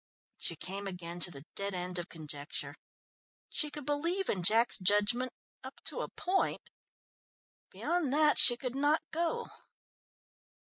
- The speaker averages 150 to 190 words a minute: No, average, 140 wpm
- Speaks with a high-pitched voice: Yes, high, 225 Hz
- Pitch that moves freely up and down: Yes, wide, 8.7 semitones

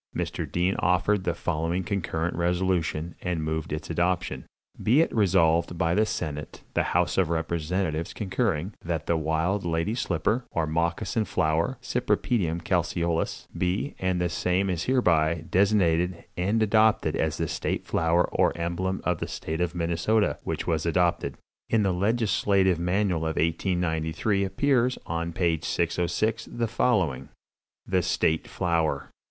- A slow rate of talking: No, average, 145 wpm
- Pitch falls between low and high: No, very low, 90 Hz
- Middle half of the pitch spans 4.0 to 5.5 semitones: No, average, 2.9 semitones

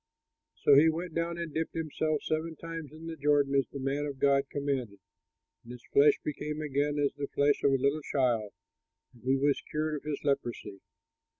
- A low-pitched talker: No, medium, 145 Hz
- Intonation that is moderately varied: No, narrow, 2.2 semitones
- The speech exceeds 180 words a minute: Yes, average, 200 wpm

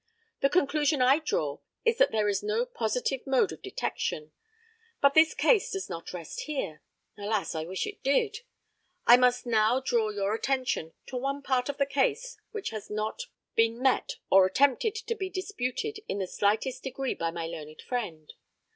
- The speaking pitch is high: Yes, very high, 255 Hz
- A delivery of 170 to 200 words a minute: Yes, average, 175 wpm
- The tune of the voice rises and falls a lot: Yes, wide, 7.0 semitones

